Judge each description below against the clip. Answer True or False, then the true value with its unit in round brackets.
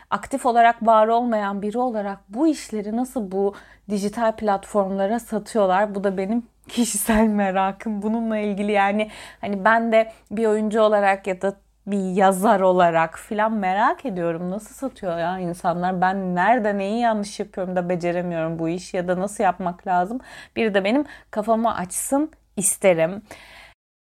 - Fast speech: True (145 wpm)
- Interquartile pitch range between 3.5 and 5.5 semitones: False (3.1 semitones)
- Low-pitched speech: False (205 Hz)